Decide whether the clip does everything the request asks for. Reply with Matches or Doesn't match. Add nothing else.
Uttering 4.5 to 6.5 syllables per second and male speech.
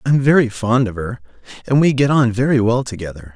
Matches